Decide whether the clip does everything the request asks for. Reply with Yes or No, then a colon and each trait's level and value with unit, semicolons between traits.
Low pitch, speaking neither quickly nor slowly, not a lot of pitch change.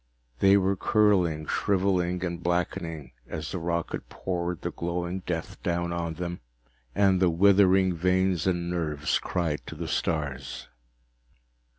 No: very low, 85 Hz; slow, 130 wpm; narrow, 2.0 semitones